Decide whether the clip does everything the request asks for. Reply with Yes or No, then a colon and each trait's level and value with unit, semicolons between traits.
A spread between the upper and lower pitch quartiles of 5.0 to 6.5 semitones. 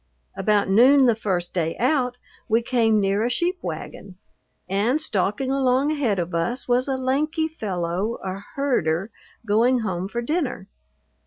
Yes: average, 5.3 semitones